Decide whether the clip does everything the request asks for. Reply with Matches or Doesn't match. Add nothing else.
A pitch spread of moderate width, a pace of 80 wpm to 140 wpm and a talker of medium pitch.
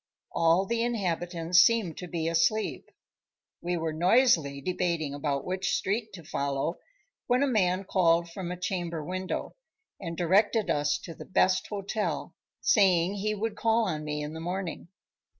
Doesn't match